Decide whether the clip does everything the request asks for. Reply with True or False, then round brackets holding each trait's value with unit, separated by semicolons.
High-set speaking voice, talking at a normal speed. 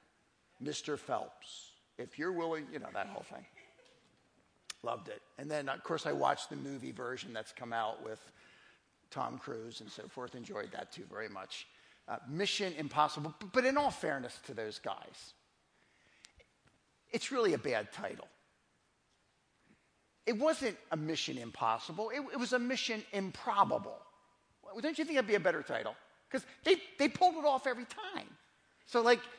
True (205 Hz; 165 wpm)